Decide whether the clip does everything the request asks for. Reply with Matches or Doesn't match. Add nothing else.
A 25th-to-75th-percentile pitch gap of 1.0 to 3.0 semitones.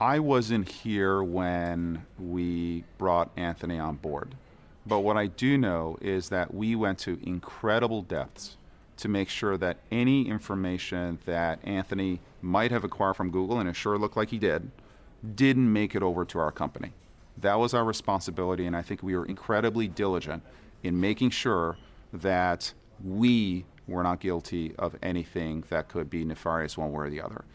Doesn't match